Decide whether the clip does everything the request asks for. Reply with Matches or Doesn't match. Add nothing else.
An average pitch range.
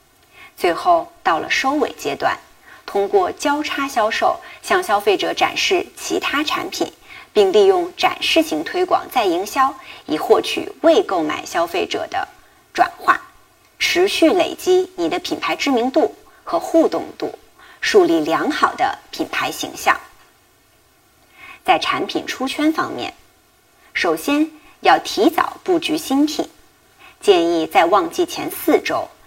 Doesn't match